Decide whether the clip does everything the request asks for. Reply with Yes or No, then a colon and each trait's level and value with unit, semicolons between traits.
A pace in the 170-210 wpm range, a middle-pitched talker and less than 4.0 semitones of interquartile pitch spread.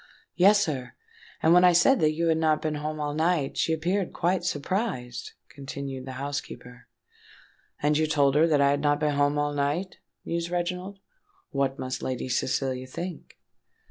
Yes: average, 175 wpm; medium, 150 Hz; average, 3.6 semitones